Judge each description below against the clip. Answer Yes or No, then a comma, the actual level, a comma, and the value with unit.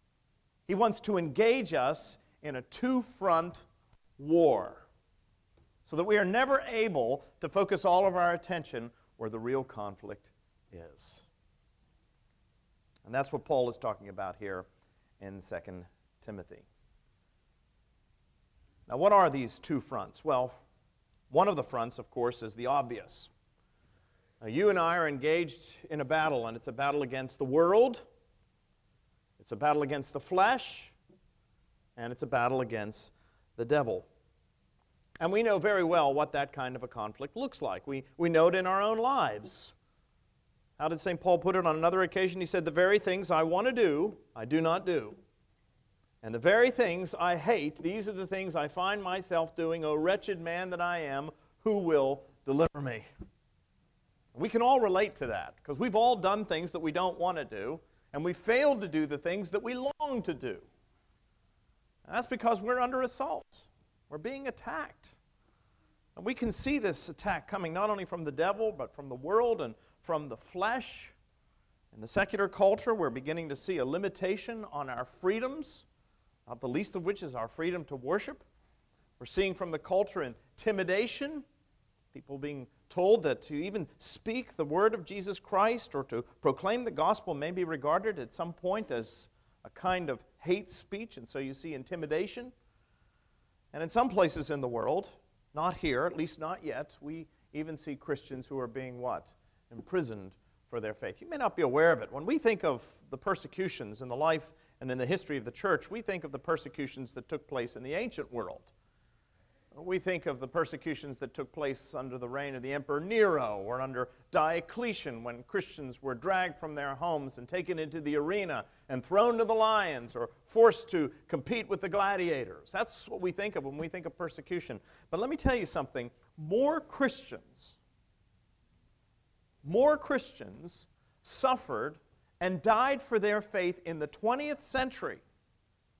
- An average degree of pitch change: No, wide, 6.9 semitones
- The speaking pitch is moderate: Yes, medium, 165 Hz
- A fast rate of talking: No, average, 180 wpm